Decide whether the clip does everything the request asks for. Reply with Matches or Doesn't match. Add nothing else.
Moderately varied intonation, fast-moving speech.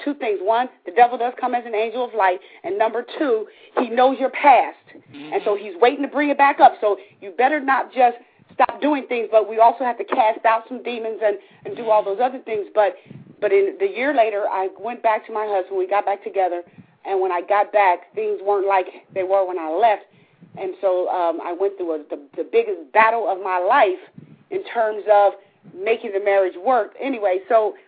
Matches